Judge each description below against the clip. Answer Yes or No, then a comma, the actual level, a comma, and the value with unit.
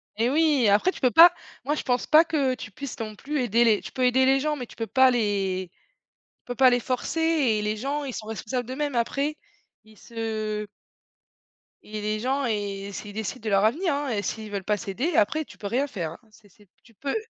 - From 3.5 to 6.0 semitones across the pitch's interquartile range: Yes, average, 4.7 semitones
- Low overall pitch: No, high, 240 Hz